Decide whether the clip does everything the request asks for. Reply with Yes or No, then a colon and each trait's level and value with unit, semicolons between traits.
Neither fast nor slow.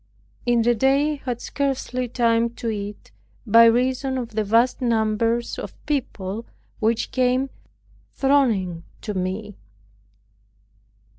No: slow, 120 wpm